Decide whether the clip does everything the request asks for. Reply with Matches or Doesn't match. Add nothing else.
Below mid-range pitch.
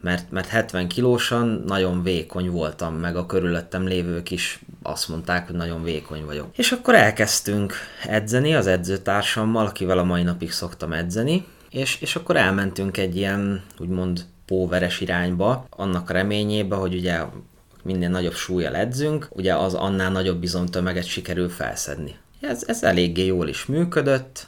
Matches